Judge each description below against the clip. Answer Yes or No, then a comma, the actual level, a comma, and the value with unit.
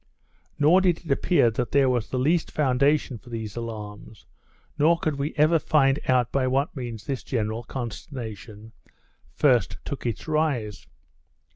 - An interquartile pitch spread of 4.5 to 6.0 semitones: Yes, average, 4.8 semitones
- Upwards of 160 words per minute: No, average, 150 wpm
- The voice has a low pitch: Yes, low, 130 Hz